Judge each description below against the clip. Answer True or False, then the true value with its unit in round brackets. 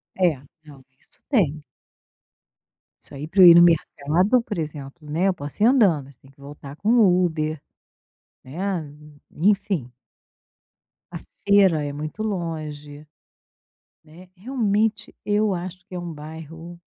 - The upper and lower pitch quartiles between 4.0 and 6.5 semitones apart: True (4.7 semitones)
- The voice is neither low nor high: True (170 Hz)